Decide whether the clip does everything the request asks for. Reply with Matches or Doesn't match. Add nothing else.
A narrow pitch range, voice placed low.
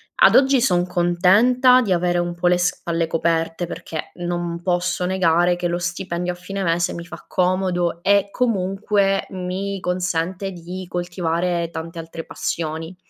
Doesn't match